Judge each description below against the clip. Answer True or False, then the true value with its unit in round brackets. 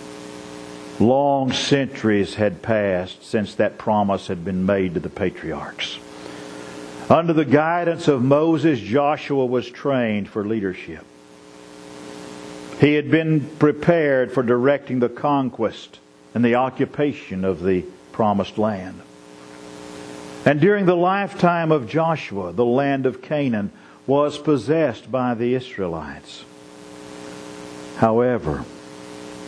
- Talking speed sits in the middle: False (110 wpm)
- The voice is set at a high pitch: False (110 Hz)